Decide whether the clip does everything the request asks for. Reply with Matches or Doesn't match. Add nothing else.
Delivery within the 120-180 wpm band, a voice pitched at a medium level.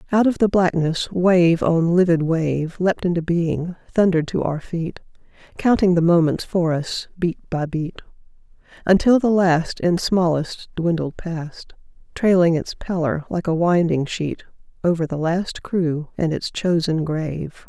Matches